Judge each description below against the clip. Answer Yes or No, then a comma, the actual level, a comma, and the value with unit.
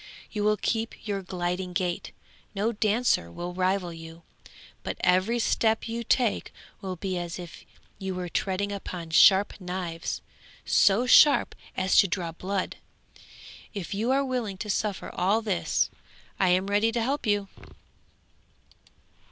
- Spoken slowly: No, average, 145 wpm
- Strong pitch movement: No, average, 3.3 semitones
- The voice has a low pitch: No, high, 195 Hz